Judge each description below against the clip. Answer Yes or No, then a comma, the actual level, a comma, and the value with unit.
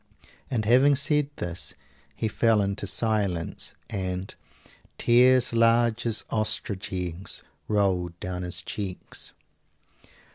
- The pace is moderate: No, slow, 105 wpm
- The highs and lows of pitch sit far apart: No, average, 4.3 semitones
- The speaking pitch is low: Yes, low, 105 Hz